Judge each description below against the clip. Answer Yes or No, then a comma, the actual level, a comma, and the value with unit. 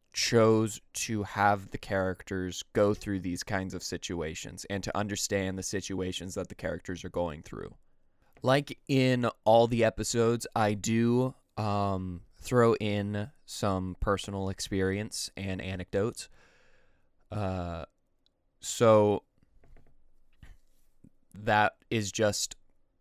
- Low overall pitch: Yes, low, 100 Hz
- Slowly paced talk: Yes, slow, 110 wpm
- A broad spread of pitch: No, average, 3.0 semitones